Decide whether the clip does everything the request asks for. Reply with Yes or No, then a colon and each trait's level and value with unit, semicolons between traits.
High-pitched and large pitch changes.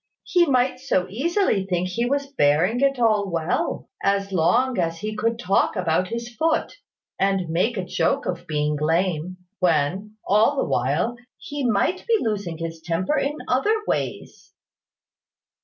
Yes: high, 200 Hz; wide, 6.3 semitones